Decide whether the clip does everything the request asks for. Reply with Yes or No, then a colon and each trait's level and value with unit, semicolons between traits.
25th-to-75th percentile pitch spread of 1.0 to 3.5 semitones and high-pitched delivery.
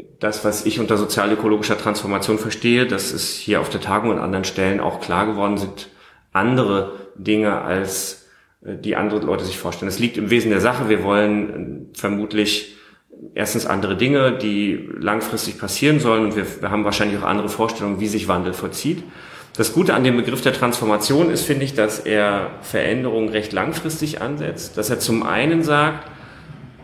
No: average, 2.8 semitones; low, 105 Hz